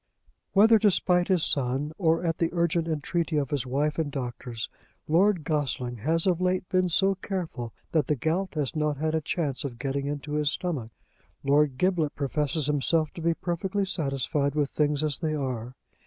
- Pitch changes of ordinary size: Yes, average, 3.6 semitones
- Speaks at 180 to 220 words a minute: Yes, average, 185 wpm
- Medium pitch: Yes, medium, 150 Hz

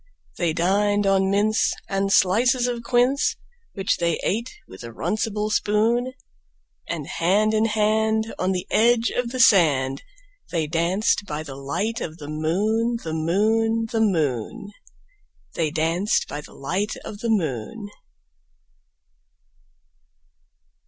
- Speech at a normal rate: No, slow, 130 wpm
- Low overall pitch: No, high, 200 Hz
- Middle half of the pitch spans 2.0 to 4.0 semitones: No, average, 5.2 semitones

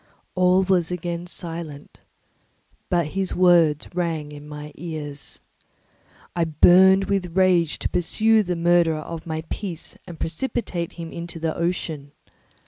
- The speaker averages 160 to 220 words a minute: No, slow, 135 wpm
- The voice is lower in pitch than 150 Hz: No, medium, 170 Hz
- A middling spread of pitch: No, narrow, 2.3 semitones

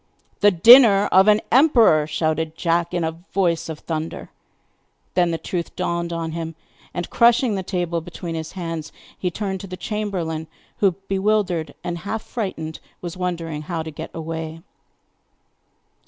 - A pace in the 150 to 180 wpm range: Yes, average, 155 wpm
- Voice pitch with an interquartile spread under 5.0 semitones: Yes, average, 3.2 semitones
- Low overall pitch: No, medium, 170 Hz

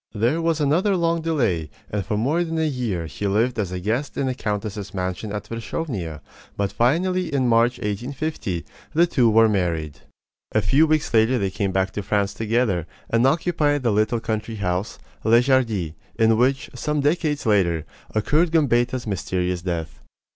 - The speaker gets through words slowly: No, average, 170 wpm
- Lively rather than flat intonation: Yes, wide, 6.3 semitones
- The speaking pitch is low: Yes, low, 115 Hz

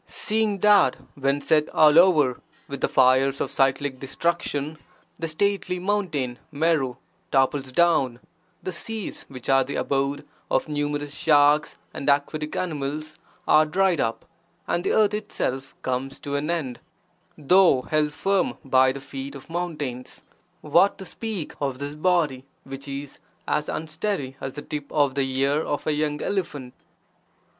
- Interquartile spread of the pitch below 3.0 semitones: No, average, 3.7 semitones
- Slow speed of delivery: No, average, 150 wpm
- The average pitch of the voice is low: No, medium, 145 Hz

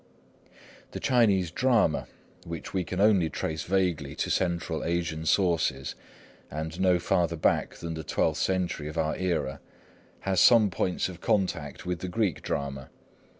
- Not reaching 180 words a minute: Yes, average, 150 wpm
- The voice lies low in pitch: Yes, very low, 85 Hz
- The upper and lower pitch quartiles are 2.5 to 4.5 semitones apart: Yes, average, 2.9 semitones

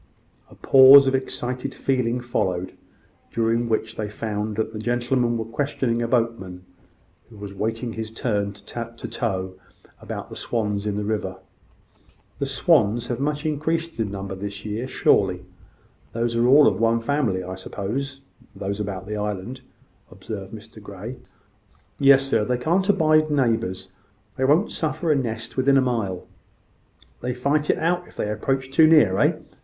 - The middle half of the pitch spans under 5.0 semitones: Yes, average, 4.4 semitones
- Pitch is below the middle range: Yes, low, 115 Hz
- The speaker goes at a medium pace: Yes, average, 160 wpm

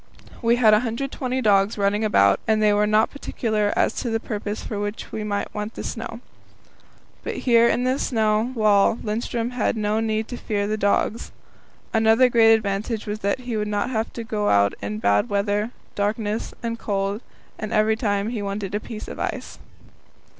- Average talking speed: Yes, average, 180 wpm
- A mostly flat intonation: Yes, narrow, 1.9 semitones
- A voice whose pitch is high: Yes, high, 215 Hz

